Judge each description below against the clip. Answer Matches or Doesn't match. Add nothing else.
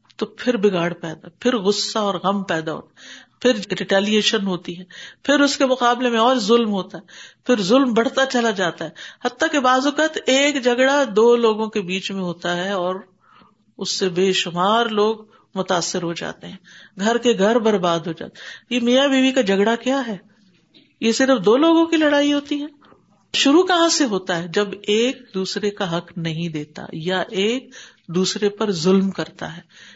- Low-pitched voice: Doesn't match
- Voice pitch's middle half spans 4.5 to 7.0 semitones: Matches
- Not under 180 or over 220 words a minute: Matches